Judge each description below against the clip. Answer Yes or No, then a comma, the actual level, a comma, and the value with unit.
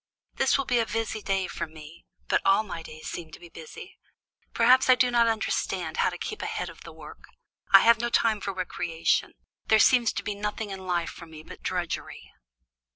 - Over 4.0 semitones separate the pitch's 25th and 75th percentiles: Yes, average, 5.1 semitones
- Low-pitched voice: No, high, 195 Hz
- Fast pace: Yes, fast, 210 wpm